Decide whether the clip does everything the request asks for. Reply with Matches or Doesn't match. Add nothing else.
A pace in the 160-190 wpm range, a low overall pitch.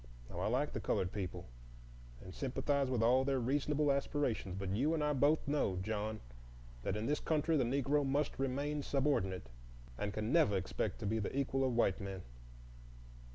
Matches